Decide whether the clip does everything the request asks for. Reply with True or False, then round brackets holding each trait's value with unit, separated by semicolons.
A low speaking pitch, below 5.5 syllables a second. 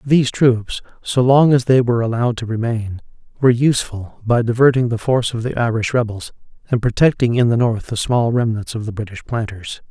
False (115 Hz; 5.7 syllables/s)